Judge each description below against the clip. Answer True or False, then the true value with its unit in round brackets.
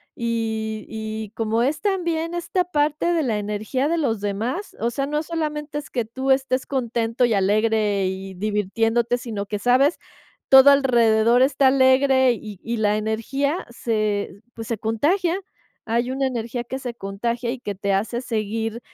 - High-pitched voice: True (235 Hz)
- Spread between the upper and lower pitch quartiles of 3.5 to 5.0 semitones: True (3.9 semitones)